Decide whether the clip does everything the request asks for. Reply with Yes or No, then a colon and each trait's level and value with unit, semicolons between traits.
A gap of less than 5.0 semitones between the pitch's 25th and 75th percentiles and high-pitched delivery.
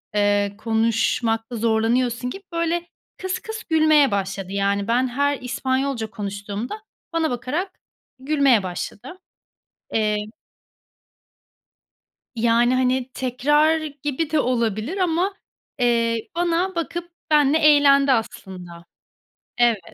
No: wide, 5.5 semitones; very high, 250 Hz